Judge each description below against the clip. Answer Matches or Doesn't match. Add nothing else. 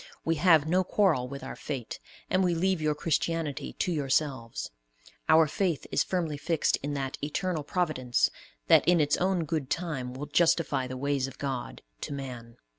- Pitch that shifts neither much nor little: Matches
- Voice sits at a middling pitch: Matches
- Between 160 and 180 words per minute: Matches